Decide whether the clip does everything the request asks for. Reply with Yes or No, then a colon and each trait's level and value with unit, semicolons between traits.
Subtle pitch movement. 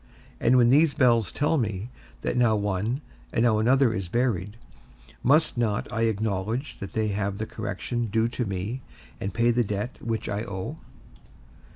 No: average, 3.0 semitones